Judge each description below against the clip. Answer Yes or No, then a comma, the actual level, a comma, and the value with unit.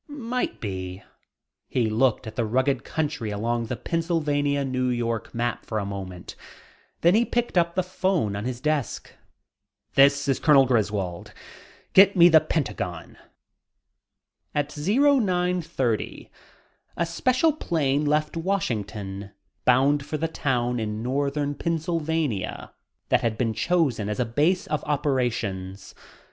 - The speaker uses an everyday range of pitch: No, wide, 6.6 semitones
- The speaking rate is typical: No, slow, 130 wpm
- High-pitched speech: No, medium, 140 Hz